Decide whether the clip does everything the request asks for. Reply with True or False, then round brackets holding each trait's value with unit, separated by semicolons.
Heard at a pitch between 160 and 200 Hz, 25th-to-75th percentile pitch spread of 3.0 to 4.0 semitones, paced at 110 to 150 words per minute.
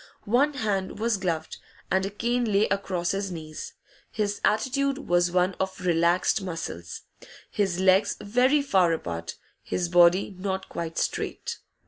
True (190 Hz; 3.4 semitones; 140 wpm)